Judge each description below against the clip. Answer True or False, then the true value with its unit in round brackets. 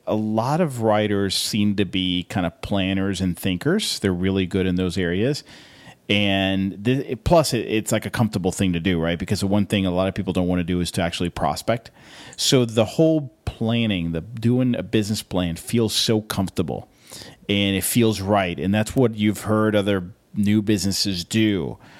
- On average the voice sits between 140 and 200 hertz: False (100 Hz)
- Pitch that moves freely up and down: False (2.8 semitones)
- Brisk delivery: False (195 wpm)